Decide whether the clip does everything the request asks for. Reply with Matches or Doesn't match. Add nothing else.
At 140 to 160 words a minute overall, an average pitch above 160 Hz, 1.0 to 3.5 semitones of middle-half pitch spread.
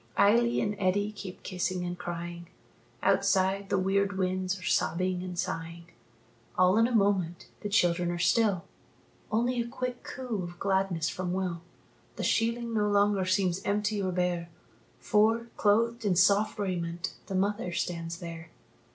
Matches